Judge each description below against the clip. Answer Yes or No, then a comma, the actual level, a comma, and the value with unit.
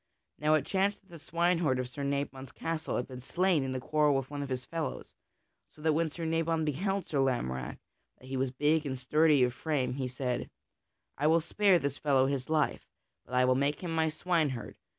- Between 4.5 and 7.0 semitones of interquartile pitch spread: No, average, 3.8 semitones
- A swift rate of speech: Yes, fast, 210 wpm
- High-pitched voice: No, medium, 145 Hz